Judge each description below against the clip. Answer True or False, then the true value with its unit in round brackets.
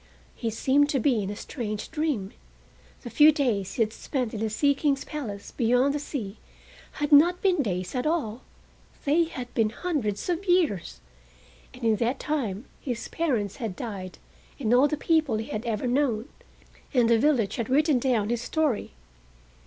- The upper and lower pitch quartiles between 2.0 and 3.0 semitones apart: False (5.3 semitones)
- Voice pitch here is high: True (250 Hz)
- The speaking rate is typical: True (175 wpm)